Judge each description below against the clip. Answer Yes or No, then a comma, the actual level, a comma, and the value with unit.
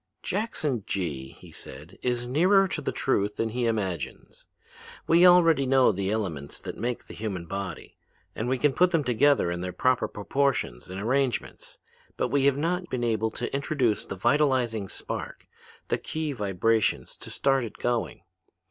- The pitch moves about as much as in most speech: No, wide, 6.0 semitones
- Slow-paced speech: No, average, 165 wpm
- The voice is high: No, low, 120 Hz